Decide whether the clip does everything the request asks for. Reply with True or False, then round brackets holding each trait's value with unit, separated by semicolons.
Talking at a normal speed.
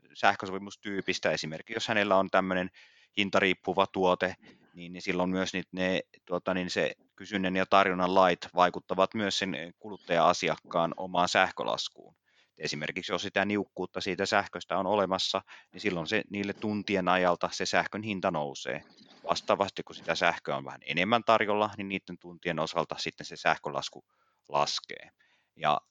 True (140 wpm)